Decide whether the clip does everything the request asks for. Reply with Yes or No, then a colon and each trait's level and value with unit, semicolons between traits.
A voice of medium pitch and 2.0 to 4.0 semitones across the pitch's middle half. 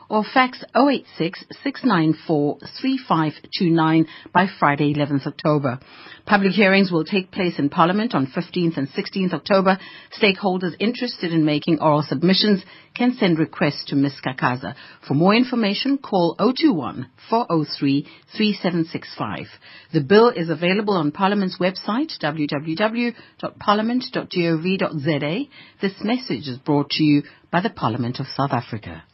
No: medium, 175 Hz; wide, 5.5 semitones